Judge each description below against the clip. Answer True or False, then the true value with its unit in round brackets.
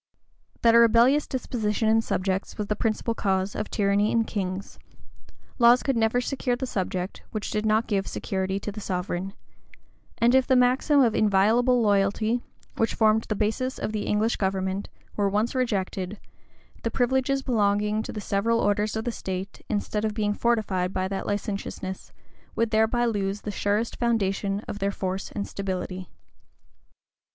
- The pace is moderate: True (160 wpm)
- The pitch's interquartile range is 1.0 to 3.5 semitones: True (2.9 semitones)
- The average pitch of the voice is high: True (210 Hz)